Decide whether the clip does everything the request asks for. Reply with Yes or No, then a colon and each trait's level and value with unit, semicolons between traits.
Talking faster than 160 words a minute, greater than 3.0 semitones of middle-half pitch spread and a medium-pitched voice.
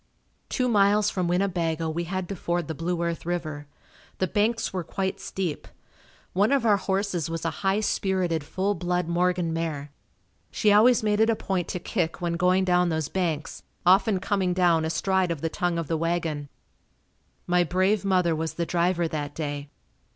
No: average, 180 wpm; narrow, 2.6 semitones; medium, 180 Hz